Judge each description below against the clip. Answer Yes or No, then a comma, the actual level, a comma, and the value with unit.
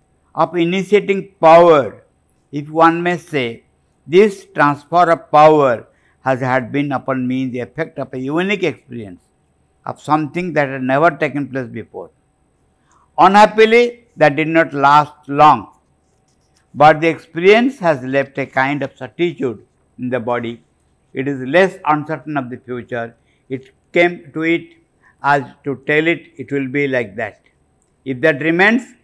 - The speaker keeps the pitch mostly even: No, average, 4.2 semitones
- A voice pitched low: No, medium, 145 Hz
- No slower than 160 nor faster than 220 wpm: No, average, 145 wpm